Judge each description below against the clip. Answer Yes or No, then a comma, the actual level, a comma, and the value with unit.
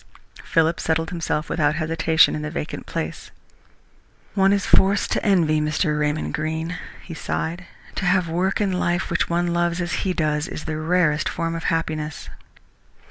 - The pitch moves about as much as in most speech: No, narrow, 2.1 semitones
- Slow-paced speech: No, average, 170 wpm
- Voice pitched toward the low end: No, medium, 165 Hz